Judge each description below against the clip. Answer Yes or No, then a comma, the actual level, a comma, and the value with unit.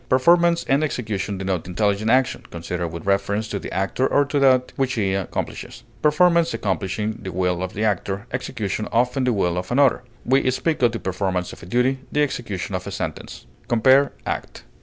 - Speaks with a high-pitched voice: No, low, 110 Hz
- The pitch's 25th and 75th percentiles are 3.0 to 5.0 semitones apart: No, wide, 5.4 semitones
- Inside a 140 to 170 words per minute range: No, average, 185 wpm